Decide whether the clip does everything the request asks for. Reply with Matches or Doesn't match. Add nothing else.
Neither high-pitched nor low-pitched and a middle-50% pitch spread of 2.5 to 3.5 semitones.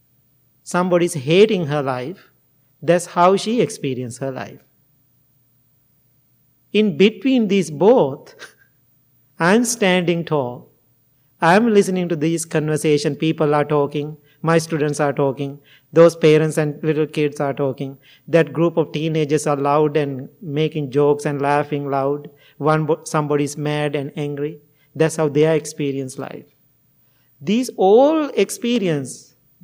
Matches